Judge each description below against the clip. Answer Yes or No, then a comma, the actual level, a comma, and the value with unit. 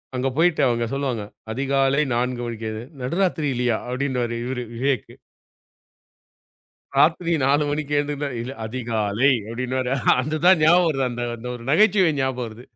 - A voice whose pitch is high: No, low, 130 Hz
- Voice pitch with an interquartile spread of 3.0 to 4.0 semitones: Yes, average, 3.4 semitones